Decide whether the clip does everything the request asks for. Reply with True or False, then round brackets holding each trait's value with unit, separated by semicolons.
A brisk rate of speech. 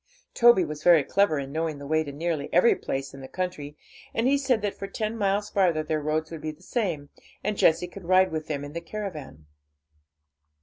True (215 wpm)